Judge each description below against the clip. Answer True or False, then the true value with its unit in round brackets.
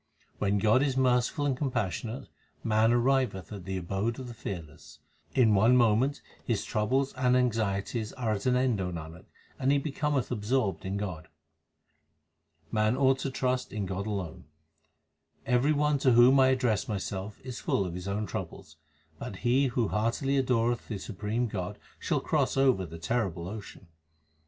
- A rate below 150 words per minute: False (165 wpm)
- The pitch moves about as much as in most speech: True (4.6 semitones)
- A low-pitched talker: True (115 Hz)